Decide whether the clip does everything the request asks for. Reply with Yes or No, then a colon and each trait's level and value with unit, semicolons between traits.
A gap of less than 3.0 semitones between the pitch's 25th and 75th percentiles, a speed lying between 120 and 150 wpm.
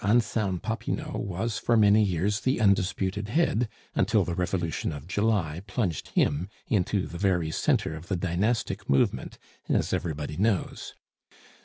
No: average, 3.8 semitones; average, 140 wpm